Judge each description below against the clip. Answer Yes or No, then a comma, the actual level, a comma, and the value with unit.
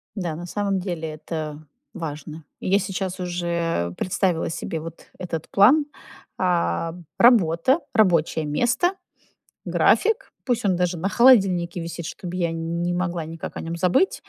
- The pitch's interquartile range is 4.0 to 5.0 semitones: No, average, 2.9 semitones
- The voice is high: No, medium, 175 Hz